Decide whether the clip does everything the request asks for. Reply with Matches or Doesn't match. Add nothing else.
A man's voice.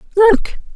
Doesn't match